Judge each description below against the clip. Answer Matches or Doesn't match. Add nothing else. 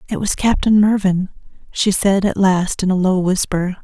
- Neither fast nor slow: Matches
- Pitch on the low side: Doesn't match